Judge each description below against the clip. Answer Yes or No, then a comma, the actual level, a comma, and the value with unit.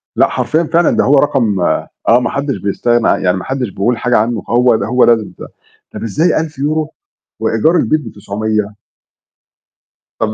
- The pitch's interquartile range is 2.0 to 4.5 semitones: No, average, 5.2 semitones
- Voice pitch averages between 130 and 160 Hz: No, low, 120 Hz